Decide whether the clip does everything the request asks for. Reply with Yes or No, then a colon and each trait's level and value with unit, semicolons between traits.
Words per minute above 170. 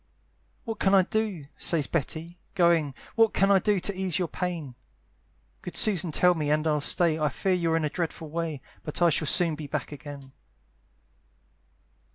Yes: average, 180 wpm